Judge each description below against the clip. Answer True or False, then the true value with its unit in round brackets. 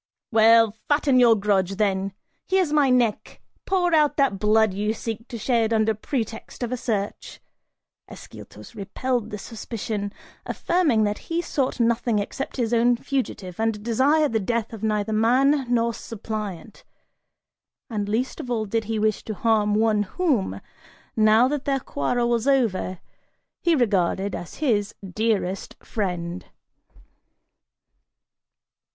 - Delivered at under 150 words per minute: True (135 wpm)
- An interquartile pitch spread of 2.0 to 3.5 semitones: True (3.2 semitones)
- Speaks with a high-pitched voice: True (225 Hz)